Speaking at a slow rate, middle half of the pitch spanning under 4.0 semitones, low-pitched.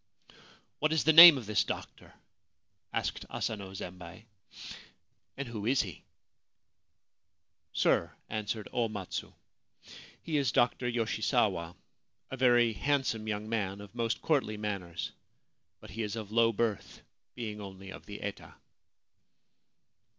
No: average, 145 wpm; average, 3.2 semitones; low, 110 Hz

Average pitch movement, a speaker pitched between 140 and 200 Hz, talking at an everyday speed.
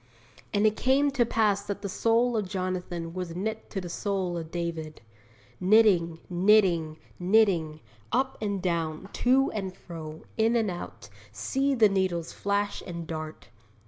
Yes: average, 4.2 semitones; high, 190 Hz; average, 150 wpm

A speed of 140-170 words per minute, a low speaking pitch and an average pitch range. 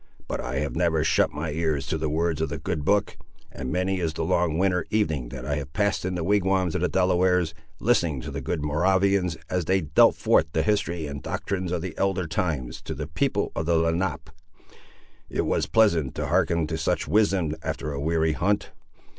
No: fast, 205 wpm; very low, 85 Hz; average, 3.3 semitones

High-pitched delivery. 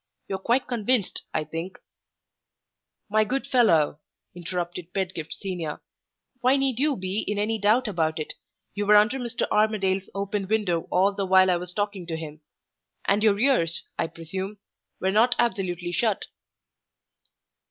Yes: high, 195 Hz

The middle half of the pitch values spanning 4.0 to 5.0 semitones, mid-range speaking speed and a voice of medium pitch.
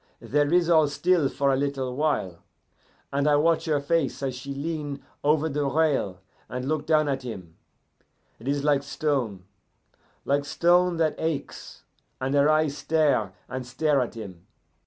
No: average, 2.8 semitones; average, 160 wpm; medium, 145 Hz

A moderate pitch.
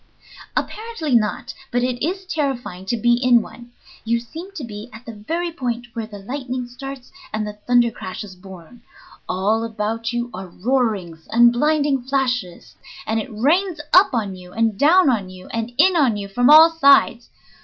No: high, 240 Hz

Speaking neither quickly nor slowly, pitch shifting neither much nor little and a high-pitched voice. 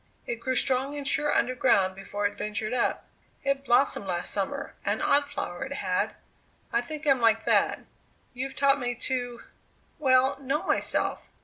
Yes: average, 170 wpm; average, 4.2 semitones; very high, 250 Hz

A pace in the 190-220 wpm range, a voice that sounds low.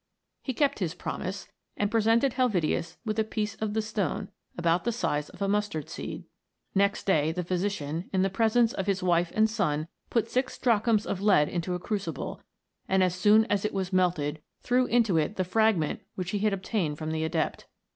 No: average, 195 wpm; high, 195 Hz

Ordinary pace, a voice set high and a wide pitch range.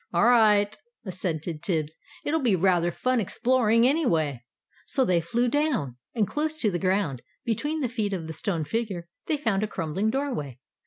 Yes: average, 170 wpm; high, 205 Hz; wide, 6.4 semitones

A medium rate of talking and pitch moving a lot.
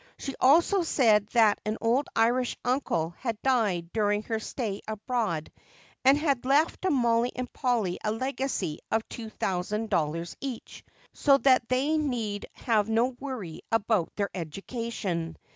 No: average, 145 wpm; average, 4.1 semitones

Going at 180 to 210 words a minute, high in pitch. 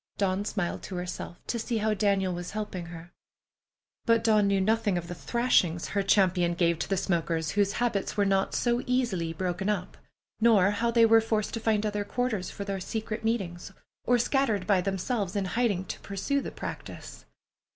Yes: average, 185 wpm; high, 200 Hz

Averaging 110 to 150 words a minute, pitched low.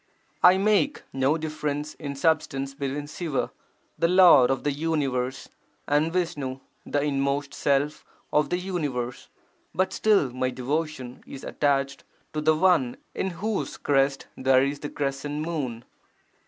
No: average, 140 wpm; medium, 145 Hz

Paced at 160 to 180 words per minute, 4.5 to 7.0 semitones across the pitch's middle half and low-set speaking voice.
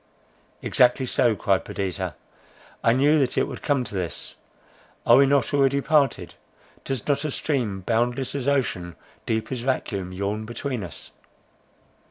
No: average, 150 wpm; wide, 5.4 semitones; low, 125 Hz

